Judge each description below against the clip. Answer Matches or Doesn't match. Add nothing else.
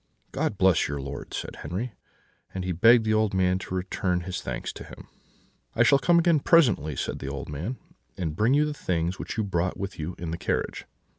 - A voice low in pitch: Matches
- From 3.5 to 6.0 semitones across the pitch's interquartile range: Matches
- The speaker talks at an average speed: Doesn't match